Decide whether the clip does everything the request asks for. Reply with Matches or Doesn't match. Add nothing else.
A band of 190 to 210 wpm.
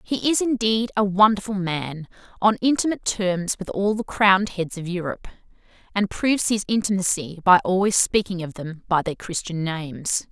Doesn't match